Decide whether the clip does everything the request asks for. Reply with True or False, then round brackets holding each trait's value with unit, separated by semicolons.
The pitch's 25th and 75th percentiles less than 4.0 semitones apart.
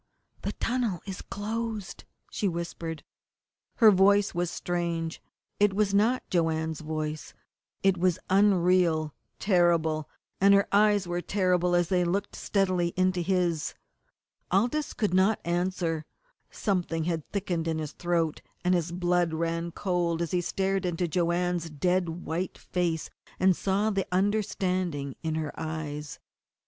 True (2.8 semitones)